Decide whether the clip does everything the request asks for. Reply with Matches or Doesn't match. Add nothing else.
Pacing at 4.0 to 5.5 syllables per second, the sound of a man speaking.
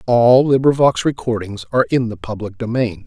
Matches